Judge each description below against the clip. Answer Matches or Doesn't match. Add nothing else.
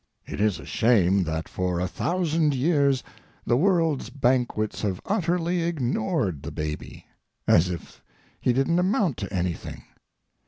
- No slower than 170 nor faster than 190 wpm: Doesn't match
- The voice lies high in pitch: Doesn't match